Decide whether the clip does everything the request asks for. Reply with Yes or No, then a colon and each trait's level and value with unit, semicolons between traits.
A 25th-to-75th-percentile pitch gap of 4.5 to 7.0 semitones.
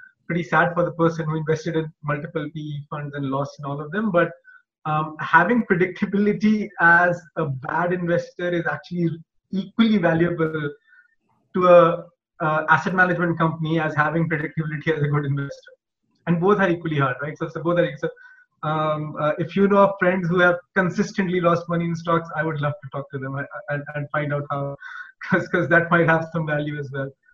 No: average, 3.1 semitones